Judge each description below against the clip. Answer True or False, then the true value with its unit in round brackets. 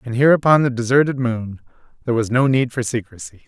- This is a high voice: False (125 Hz)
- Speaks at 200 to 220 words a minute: True (205 wpm)